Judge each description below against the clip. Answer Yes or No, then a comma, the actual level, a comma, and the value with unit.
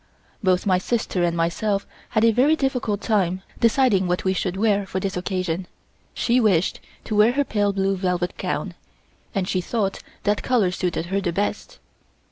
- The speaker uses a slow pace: No, average, 175 wpm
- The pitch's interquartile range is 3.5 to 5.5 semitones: No, average, 3.1 semitones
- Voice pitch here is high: Yes, high, 195 Hz